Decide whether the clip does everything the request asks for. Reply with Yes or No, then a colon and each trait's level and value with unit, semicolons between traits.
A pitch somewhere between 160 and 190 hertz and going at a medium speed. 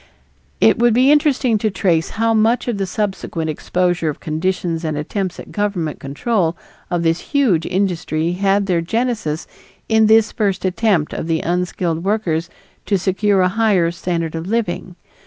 Yes: medium, 185 Hz; average, 160 wpm